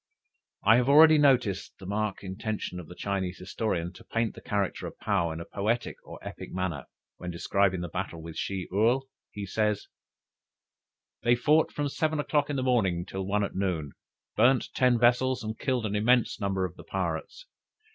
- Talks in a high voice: No, low, 105 Hz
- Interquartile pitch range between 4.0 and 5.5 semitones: Yes, average, 4.8 semitones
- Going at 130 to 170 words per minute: No, average, 185 wpm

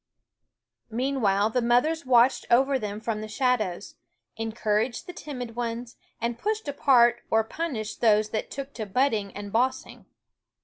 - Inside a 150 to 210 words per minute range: No, average, 140 wpm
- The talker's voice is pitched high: Yes, high, 235 Hz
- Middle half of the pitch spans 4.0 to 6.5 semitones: No, average, 3.3 semitones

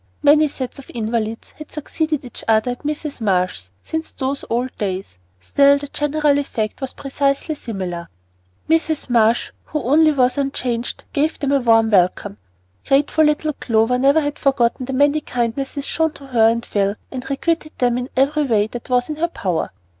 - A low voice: No, very high, 265 Hz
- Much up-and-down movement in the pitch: No, average, 4.3 semitones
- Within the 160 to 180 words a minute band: Yes, average, 175 wpm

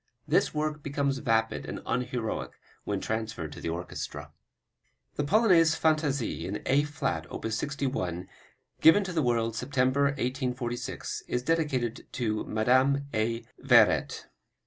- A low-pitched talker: Yes, low, 130 Hz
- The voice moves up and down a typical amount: Yes, average, 4.3 semitones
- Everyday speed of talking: No, slow, 125 wpm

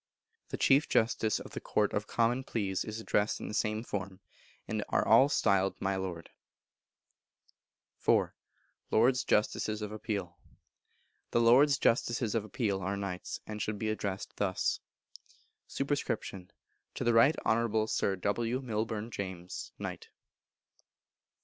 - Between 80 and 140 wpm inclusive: Yes, slow, 135 wpm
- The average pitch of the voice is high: No, low, 110 Hz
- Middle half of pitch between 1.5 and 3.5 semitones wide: Yes, average, 2.9 semitones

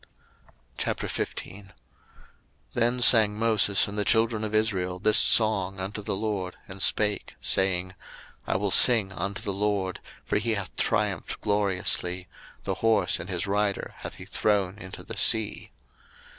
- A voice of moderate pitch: No, low, 100 Hz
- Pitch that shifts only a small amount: Yes, narrow, 2.1 semitones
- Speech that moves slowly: No, average, 145 wpm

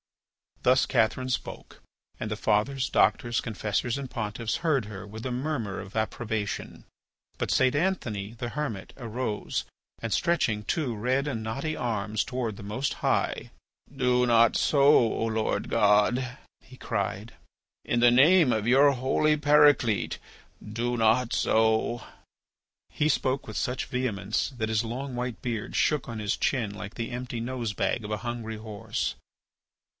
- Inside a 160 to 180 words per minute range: No, average, 150 wpm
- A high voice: No, low, 120 Hz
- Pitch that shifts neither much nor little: Yes, average, 3.0 semitones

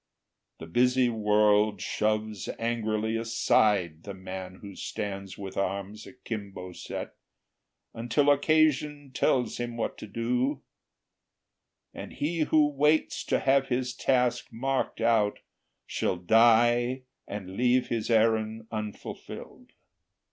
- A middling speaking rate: No, slow, 110 wpm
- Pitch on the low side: Yes, low, 115 Hz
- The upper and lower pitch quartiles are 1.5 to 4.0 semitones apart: Yes, average, 3.4 semitones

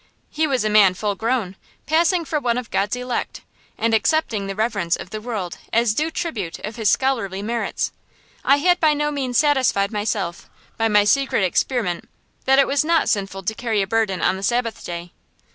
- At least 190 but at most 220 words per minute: Yes, average, 195 wpm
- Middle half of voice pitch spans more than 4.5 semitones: Yes, average, 5.3 semitones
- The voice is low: No, high, 225 Hz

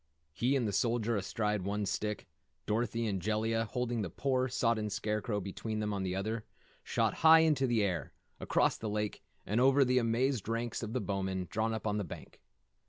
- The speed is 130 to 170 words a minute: No, average, 185 wpm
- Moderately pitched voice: No, low, 110 Hz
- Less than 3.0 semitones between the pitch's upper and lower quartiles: Yes, narrow, 2.6 semitones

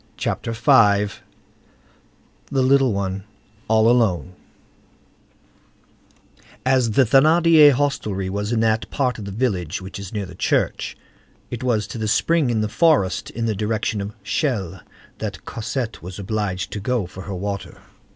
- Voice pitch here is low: Yes, low, 110 Hz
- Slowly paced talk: No, average, 145 wpm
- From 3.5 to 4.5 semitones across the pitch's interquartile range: Yes, average, 4.1 semitones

